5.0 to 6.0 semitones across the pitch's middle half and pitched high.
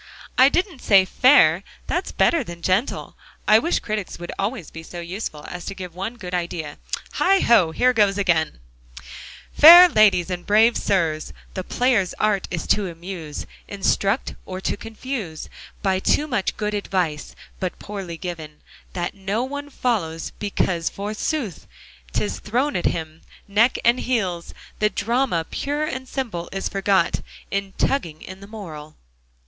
Yes: average, 5.3 semitones; high, 195 Hz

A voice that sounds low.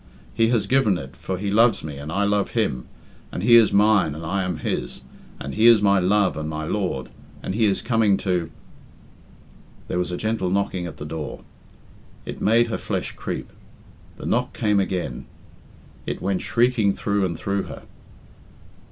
Yes: low, 100 Hz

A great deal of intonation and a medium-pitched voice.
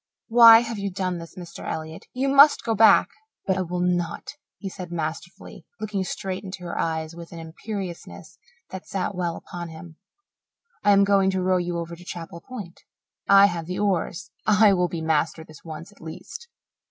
No: average, 2.9 semitones; medium, 180 Hz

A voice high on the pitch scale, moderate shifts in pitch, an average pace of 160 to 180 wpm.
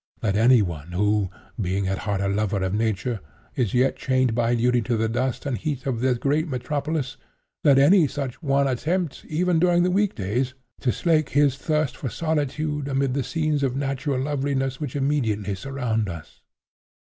No: low, 130 Hz; average, 4.7 semitones; average, 170 wpm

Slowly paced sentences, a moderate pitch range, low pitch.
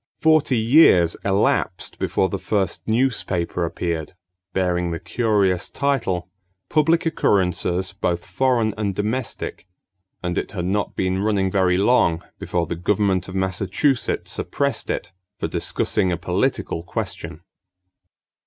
Yes: slow, 125 wpm; average, 3.8 semitones; very low, 95 Hz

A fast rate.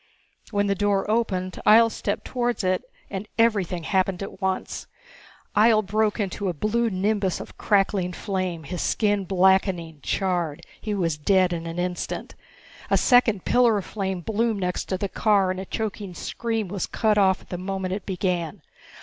No: average, 170 wpm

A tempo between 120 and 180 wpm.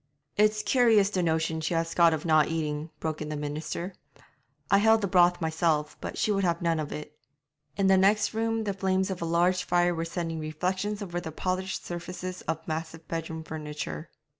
No: average, 195 wpm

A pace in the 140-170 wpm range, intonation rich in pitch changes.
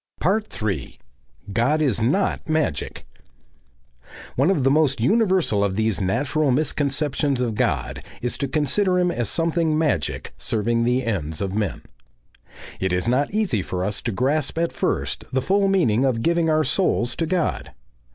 Yes: average, 155 wpm; wide, 6.5 semitones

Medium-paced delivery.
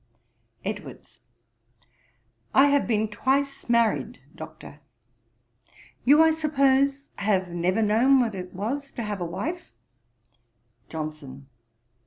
No: slow, 105 wpm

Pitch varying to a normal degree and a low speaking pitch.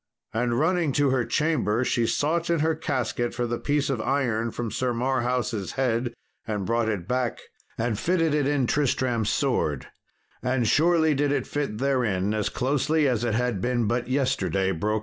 Yes: average, 3.9 semitones; low, 125 Hz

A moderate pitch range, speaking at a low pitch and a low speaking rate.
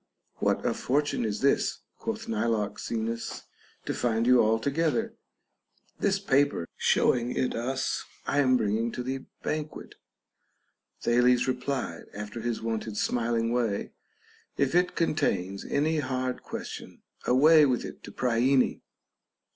Yes: average, 3.8 semitones; low, 125 Hz; slow, 130 wpm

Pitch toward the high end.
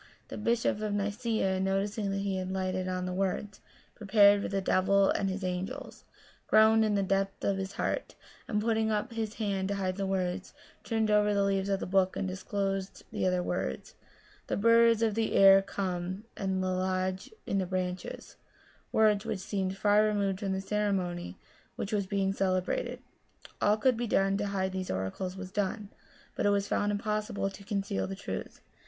Yes: high, 195 Hz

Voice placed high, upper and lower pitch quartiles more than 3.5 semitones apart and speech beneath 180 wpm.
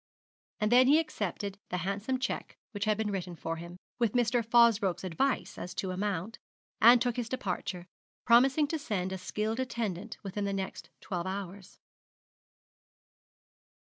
Yes: high, 210 Hz; average, 4.2 semitones; average, 150 wpm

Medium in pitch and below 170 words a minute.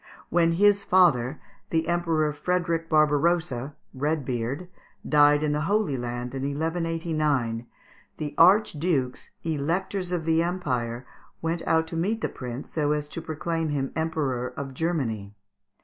Yes: medium, 155 Hz; slow, 135 wpm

